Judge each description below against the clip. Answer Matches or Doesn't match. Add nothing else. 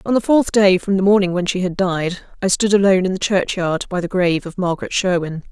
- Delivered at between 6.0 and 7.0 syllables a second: Matches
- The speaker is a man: Doesn't match